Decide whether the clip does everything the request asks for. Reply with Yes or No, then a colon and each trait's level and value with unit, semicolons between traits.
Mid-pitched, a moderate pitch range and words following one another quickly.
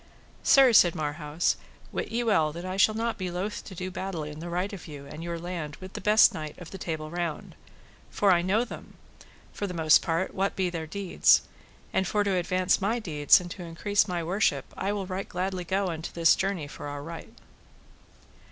Yes: medium, 180 Hz; average, 3.2 semitones; fast, 210 wpm